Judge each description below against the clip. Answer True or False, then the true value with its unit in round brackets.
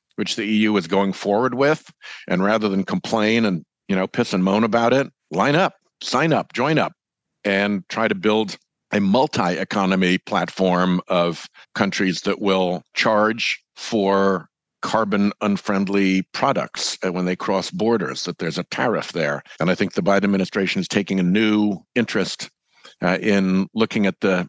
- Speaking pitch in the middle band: False (100 Hz)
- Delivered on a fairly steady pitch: True (2.2 semitones)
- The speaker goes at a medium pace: True (160 wpm)